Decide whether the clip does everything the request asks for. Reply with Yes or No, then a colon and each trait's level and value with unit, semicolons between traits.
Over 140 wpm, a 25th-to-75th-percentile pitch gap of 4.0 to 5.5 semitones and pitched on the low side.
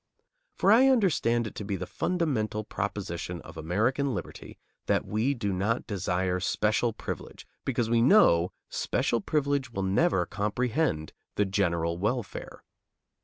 No: slow, 135 wpm; average, 5.2 semitones; low, 105 Hz